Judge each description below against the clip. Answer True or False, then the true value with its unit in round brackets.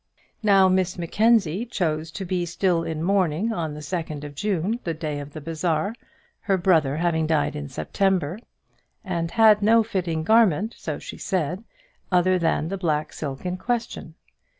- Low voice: False (175 Hz)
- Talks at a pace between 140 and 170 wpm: True (165 wpm)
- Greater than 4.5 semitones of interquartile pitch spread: False (3.8 semitones)